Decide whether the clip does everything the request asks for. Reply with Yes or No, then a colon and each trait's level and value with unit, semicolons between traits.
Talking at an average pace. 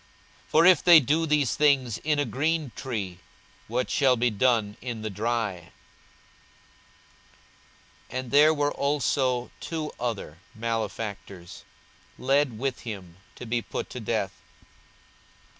No: slow, 130 wpm